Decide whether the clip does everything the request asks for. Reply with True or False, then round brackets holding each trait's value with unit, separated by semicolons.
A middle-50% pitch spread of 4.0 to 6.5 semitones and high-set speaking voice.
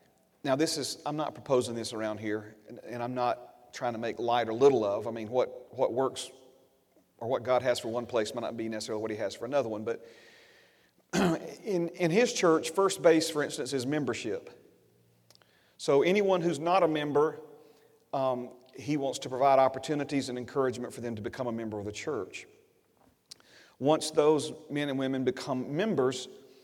False (4.7 semitones; 135 Hz)